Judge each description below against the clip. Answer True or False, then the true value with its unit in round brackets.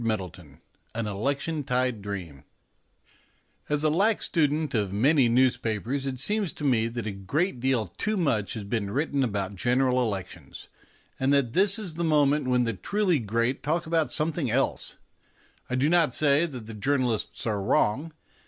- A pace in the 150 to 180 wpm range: True (165 wpm)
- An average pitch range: False (5.8 semitones)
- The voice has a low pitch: True (130 Hz)